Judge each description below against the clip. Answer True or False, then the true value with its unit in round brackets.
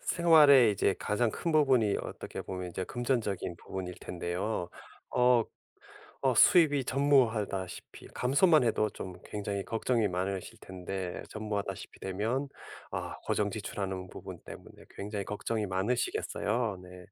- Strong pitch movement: False (4.7 semitones)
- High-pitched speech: False (105 Hz)